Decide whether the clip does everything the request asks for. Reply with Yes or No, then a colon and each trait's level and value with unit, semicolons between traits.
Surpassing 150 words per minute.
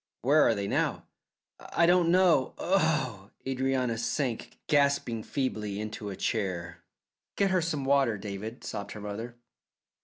No: average, 140 wpm